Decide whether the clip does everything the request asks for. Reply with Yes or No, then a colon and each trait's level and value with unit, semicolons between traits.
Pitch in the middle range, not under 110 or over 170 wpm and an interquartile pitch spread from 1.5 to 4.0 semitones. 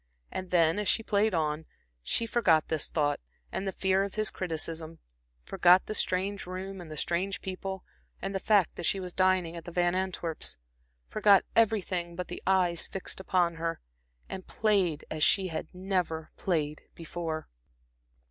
Yes: medium, 180 Hz; average, 165 wpm; average, 2.7 semitones